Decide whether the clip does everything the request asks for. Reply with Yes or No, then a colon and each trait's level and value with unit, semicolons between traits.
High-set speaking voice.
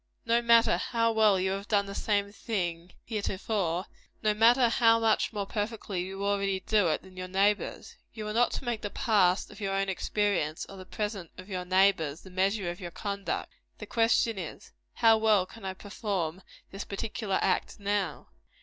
Yes: high, 200 Hz